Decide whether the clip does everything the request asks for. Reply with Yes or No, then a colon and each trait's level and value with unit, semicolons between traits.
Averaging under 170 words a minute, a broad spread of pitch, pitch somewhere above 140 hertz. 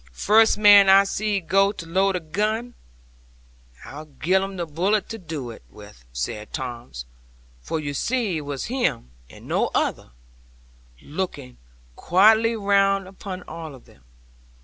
Yes: average, 150 wpm; wide, 5.7 semitones; medium, 185 Hz